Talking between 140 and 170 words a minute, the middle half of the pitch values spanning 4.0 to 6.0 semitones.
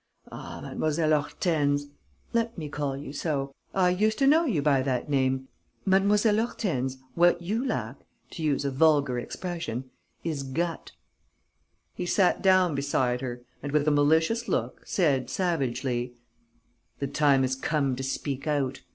Yes: average, 150 wpm; average, 4.7 semitones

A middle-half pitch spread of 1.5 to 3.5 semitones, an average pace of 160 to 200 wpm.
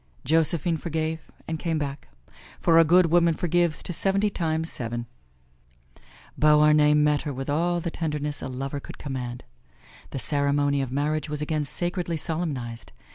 No: average, 2.7 semitones; average, 150 wpm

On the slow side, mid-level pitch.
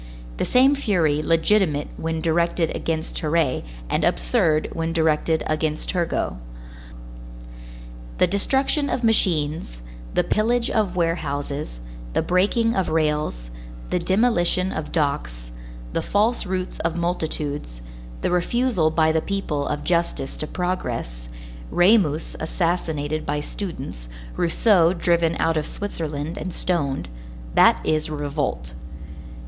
Yes: slow, 115 wpm; medium, 165 Hz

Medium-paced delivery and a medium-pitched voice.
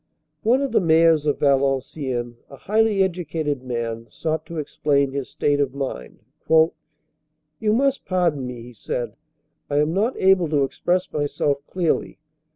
Yes: average, 150 wpm; medium, 150 Hz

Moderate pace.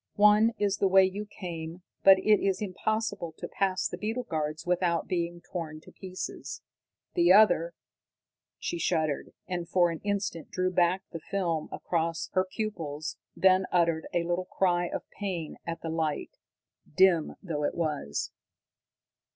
Yes: average, 160 wpm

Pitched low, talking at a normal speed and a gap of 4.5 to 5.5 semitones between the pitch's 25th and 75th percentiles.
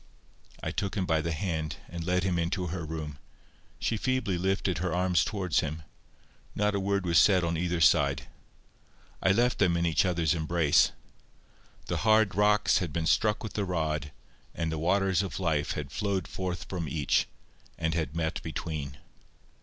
No: very low, 85 Hz; average, 175 wpm; average, 3.3 semitones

